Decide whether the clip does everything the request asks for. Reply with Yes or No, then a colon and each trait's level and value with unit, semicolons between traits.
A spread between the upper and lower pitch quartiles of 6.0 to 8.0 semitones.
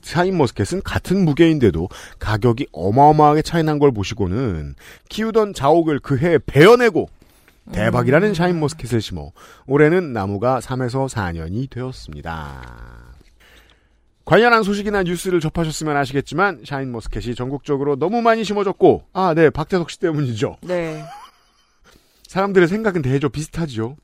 Yes: wide, 6.7 semitones